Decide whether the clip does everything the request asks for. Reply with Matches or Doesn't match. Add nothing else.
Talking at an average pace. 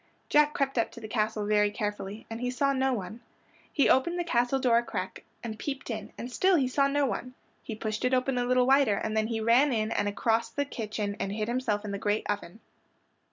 Doesn't match